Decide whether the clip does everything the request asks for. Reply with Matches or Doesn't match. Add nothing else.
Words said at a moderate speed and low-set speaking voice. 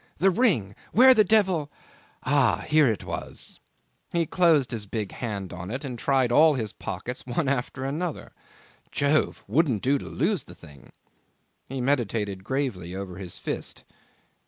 Matches